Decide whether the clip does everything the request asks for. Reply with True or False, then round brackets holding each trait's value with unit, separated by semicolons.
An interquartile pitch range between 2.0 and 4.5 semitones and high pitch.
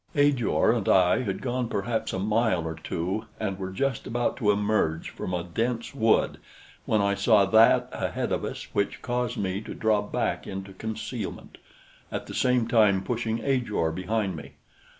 False (3.7 semitones; 110 Hz)